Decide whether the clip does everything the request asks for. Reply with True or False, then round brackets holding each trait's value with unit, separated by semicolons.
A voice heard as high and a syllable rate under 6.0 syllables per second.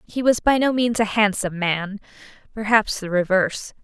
True (210 Hz; 5.2 syllables/s)